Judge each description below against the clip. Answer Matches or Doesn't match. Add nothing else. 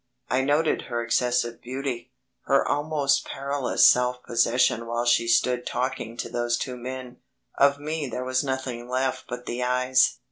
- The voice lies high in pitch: Doesn't match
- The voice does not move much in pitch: Matches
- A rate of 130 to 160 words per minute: Matches